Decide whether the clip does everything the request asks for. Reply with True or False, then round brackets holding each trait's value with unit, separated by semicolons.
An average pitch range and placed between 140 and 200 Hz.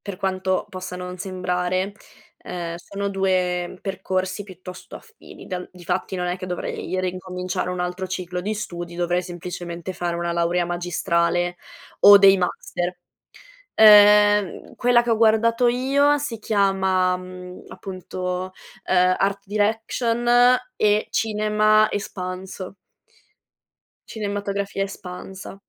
False (2.3 semitones; 185 Hz)